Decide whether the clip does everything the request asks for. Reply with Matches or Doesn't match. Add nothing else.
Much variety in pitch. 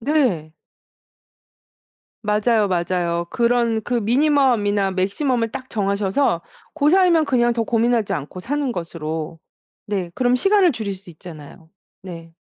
Matches